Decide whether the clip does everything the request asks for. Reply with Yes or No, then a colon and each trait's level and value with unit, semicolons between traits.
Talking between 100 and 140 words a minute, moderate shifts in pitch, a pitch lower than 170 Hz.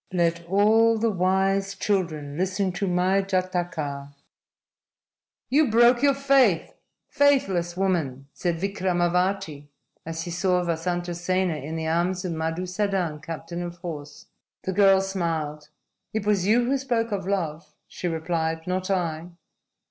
No: slow, 135 wpm; average, 3.0 semitones; medium, 180 Hz